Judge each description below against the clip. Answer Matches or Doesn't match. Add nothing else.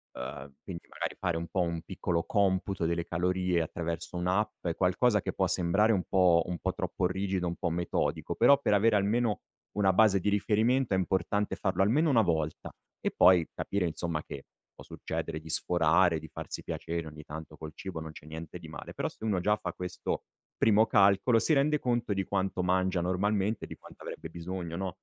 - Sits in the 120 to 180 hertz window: Doesn't match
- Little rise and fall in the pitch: Doesn't match